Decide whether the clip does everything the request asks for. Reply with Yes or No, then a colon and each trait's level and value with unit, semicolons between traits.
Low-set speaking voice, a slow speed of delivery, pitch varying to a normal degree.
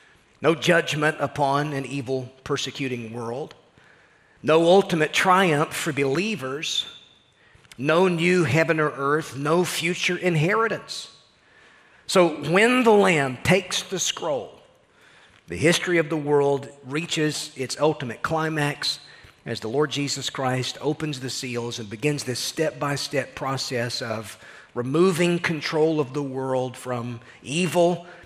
No: medium, 150 Hz; slow, 125 wpm; average, 4.3 semitones